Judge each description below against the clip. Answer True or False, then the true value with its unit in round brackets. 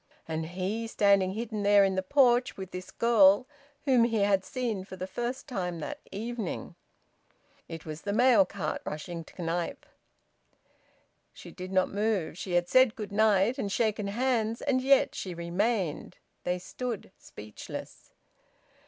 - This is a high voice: True (200 Hz)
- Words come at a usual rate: True (155 wpm)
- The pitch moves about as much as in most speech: True (4.1 semitones)